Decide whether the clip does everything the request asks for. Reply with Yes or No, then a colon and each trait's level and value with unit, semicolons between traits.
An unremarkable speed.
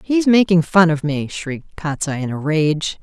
No: fast, 220 wpm